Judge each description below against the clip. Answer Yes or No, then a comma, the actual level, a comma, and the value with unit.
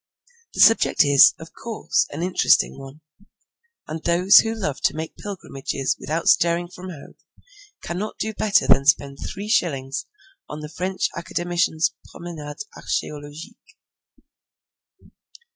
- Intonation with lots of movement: No, average, 4.2 semitones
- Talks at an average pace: No, slow, 125 wpm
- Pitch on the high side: No, medium, 170 Hz